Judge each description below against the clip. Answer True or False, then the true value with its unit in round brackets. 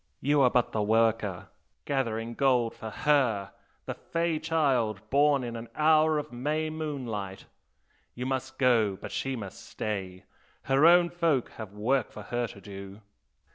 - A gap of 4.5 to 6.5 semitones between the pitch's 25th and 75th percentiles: True (5.2 semitones)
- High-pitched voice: False (125 Hz)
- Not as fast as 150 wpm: False (155 wpm)